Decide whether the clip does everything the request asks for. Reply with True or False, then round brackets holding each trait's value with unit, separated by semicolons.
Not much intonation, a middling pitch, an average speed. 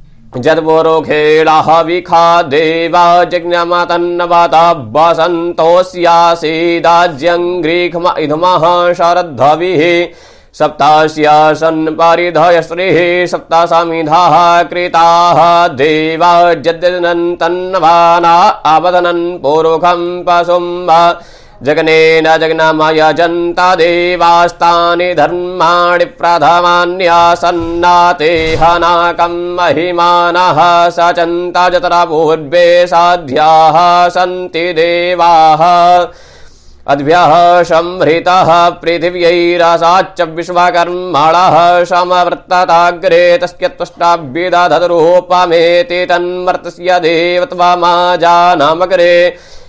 False (1.0 semitones; 175 Hz; 55 wpm)